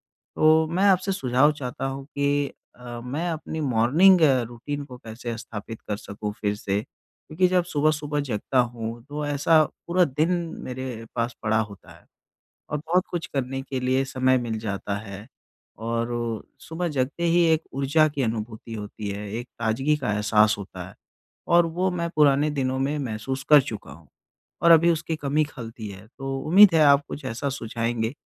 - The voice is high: No, low, 135 Hz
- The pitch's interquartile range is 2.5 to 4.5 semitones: No, average, 5.3 semitones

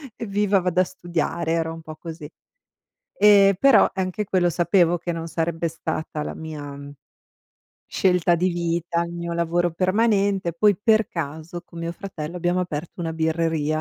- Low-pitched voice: No, medium, 170 Hz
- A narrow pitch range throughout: Yes, narrow, 2.2 semitones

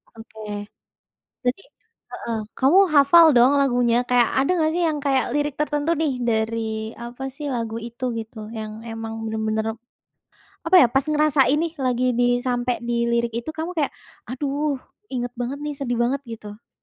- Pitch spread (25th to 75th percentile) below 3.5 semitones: No, average, 3.9 semitones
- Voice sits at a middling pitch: No, very high, 250 Hz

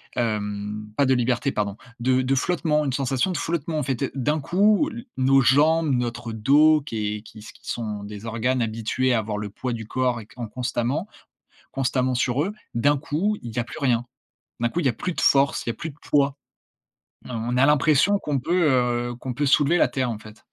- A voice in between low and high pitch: No, low, 130 Hz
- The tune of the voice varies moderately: Yes, average, 4.1 semitones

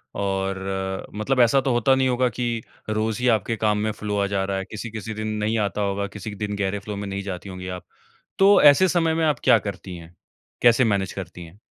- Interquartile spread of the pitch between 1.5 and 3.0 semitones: No, average, 3.4 semitones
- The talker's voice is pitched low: Yes, low, 105 Hz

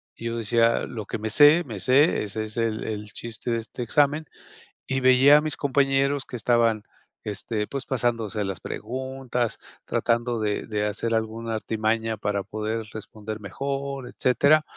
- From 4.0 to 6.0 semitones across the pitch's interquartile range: No, average, 3.5 semitones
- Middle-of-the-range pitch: No, low, 115 Hz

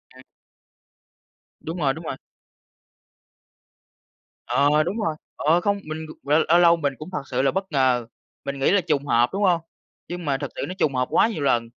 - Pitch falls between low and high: Yes, medium, 155 Hz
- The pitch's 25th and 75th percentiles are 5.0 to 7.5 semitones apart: No, average, 4.3 semitones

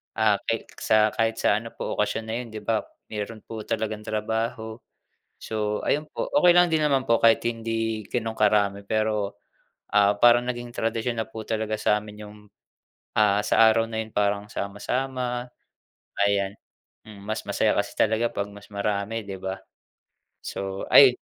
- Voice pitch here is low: Yes, low, 110 Hz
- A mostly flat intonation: Yes, narrow, 1.7 semitones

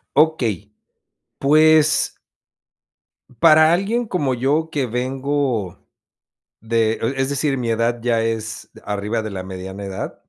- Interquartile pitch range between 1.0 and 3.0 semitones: No, average, 5.1 semitones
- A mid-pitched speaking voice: No, low, 125 Hz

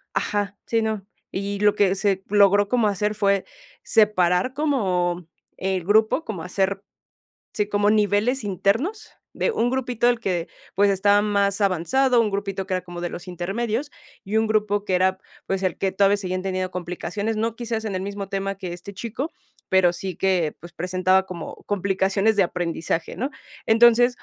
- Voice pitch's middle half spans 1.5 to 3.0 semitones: Yes, average, 2.7 semitones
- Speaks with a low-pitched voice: No, high, 200 Hz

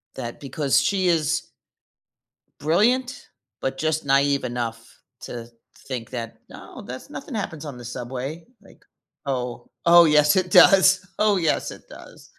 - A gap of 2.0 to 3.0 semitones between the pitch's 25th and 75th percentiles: No, wide, 5.6 semitones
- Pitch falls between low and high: Yes, medium, 145 Hz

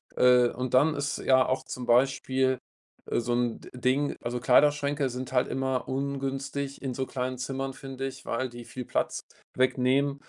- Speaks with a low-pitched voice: Yes, low, 130 Hz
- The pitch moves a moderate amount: No, narrow, 1.5 semitones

